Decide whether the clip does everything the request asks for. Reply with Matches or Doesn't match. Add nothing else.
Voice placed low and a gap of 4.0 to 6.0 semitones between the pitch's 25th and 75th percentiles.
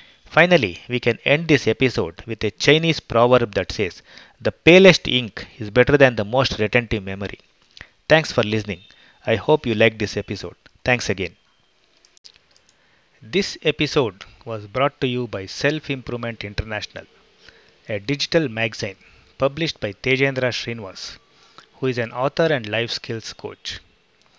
Matches